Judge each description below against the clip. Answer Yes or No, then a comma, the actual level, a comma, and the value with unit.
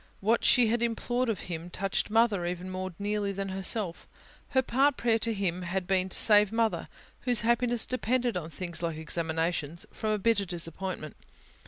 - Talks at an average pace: Yes, average, 175 wpm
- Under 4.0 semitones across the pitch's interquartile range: No, average, 4.5 semitones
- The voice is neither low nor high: No, high, 200 Hz